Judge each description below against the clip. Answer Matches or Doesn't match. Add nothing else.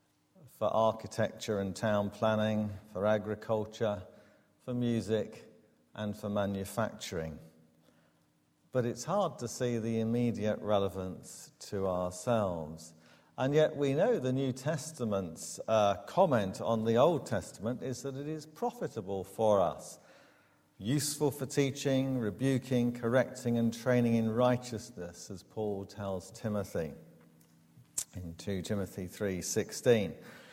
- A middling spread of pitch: Matches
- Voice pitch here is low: Matches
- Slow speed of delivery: Matches